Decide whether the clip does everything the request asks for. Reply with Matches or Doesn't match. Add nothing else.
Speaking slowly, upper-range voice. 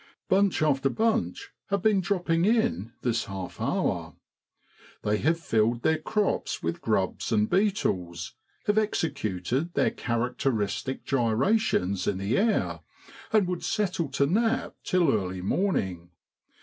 Doesn't match